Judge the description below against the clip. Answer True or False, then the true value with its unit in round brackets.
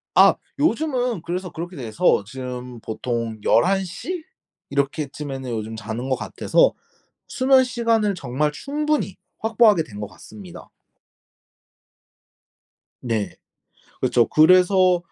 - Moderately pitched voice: True (155 Hz)